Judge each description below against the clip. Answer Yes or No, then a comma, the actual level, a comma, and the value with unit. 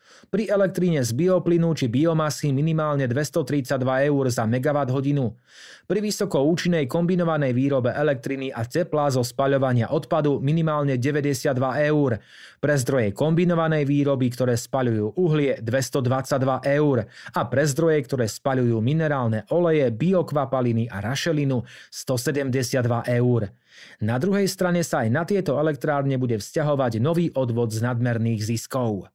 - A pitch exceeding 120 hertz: Yes, medium, 140 Hz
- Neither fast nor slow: Yes, average, 125 wpm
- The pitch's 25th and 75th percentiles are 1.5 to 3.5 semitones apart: No, average, 3.9 semitones